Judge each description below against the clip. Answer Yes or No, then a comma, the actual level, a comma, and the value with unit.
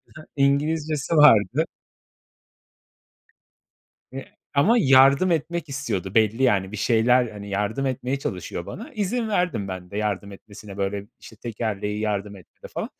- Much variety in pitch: Yes, wide, 6.3 semitones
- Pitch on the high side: No, low, 120 Hz